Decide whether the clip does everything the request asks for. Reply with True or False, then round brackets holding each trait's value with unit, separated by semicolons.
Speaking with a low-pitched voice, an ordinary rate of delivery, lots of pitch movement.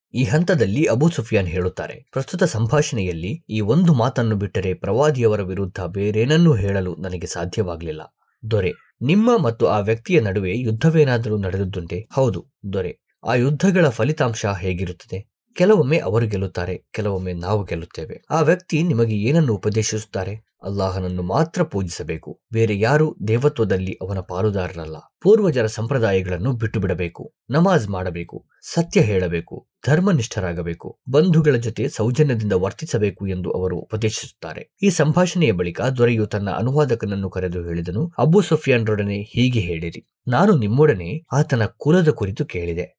False (110 Hz; 115 wpm; 7.8 semitones)